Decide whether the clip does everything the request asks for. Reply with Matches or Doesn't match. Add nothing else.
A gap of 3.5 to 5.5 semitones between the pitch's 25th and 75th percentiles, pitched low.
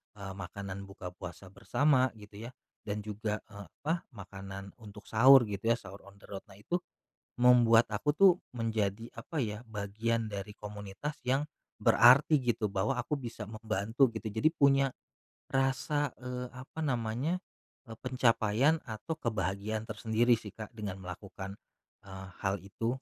Matches